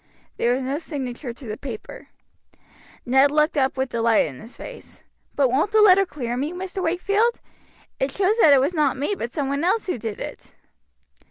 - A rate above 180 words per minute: Yes, average, 195 wpm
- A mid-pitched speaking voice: No, very high, 280 Hz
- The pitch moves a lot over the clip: Yes, wide, 6.3 semitones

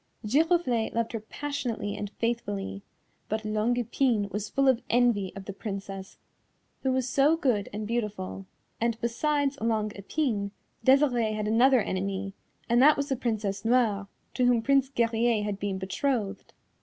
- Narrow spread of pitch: No, average, 4.0 semitones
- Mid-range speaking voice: No, high, 230 Hz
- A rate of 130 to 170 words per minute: Yes, average, 155 wpm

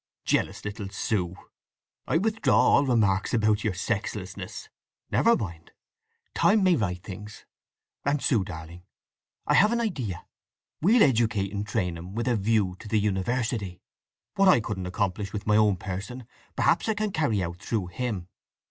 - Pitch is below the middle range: Yes, low, 105 Hz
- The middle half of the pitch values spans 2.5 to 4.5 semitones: No, average, 4.9 semitones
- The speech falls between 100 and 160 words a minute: Yes, average, 155 wpm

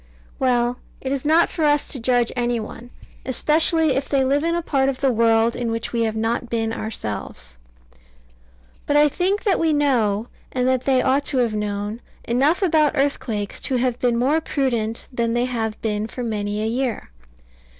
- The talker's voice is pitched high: Yes, high, 245 Hz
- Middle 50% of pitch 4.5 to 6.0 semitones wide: No, average, 3.7 semitones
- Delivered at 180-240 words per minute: Yes, average, 190 wpm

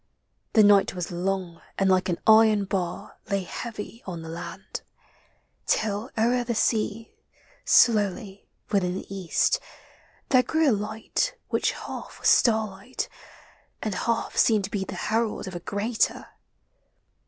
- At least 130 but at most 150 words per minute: Yes, average, 140 wpm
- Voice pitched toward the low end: No, high, 205 Hz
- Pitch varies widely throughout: No, average, 2.9 semitones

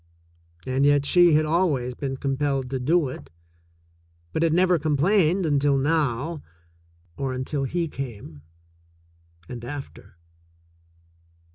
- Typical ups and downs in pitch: Yes, average, 3.8 semitones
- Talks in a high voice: No, medium, 140 Hz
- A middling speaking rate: No, slow, 125 wpm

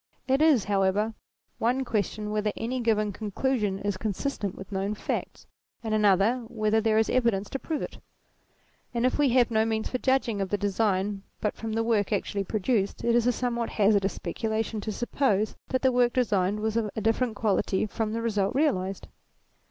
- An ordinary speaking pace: Yes, average, 190 wpm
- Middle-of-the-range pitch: No, high, 220 Hz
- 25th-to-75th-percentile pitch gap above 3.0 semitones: No, average, 2.7 semitones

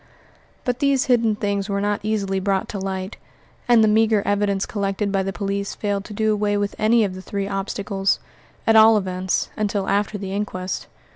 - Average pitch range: No, narrow, 1.6 semitones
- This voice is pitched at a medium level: No, high, 205 Hz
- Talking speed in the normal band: Yes, average, 195 wpm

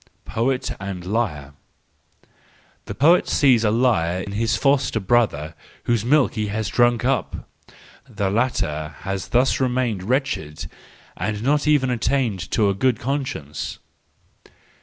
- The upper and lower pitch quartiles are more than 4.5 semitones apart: Yes, average, 4.9 semitones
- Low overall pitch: Yes, low, 115 Hz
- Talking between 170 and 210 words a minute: No, slow, 135 wpm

